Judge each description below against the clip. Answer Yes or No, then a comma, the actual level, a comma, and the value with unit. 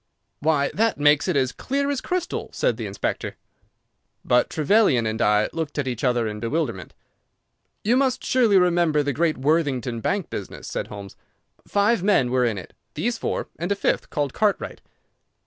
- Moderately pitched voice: Yes, medium, 150 Hz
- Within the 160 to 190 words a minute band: Yes, average, 165 wpm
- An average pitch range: No, wide, 8.4 semitones